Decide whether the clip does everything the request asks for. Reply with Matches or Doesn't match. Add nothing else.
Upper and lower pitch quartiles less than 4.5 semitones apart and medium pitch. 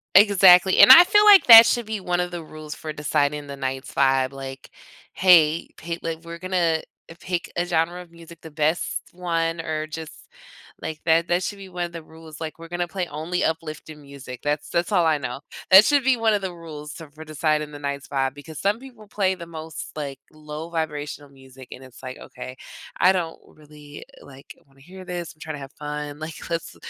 Matches